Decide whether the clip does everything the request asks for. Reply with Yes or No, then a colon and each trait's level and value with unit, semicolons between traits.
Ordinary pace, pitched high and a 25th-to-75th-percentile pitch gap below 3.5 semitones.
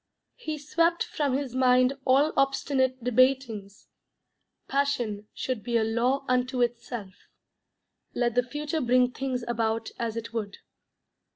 No: slow, 125 wpm; very high, 250 Hz; average, 2.7 semitones